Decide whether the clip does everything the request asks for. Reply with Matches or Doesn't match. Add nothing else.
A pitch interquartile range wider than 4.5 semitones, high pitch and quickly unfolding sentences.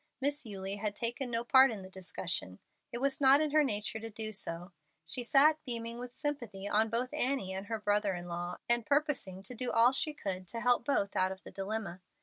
Matches